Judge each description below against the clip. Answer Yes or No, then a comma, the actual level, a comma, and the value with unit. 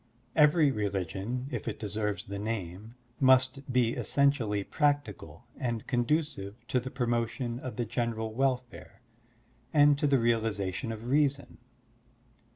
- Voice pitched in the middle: No, low, 120 Hz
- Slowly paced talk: Yes, slow, 125 wpm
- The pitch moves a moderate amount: Yes, average, 4.2 semitones